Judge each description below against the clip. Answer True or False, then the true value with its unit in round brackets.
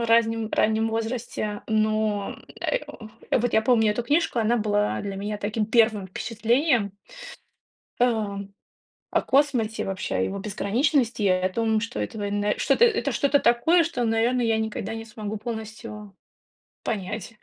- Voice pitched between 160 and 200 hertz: False (220 Hz)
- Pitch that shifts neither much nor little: False (2.2 semitones)